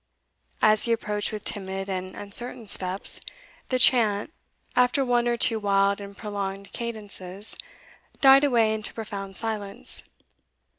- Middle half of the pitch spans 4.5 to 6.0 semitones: No, average, 2.9 semitones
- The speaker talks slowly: Yes, slow, 130 wpm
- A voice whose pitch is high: Yes, high, 210 Hz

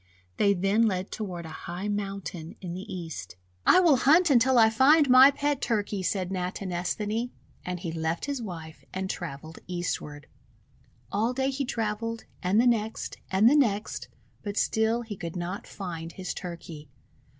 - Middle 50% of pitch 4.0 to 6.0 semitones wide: Yes, average, 4.7 semitones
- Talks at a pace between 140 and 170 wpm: Yes, average, 160 wpm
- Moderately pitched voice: No, high, 200 Hz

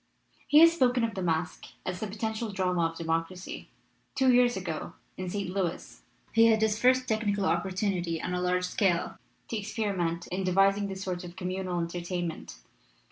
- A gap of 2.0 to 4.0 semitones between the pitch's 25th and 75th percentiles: Yes, average, 3.5 semitones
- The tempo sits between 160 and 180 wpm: Yes, average, 175 wpm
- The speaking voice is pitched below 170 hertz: No, high, 190 Hz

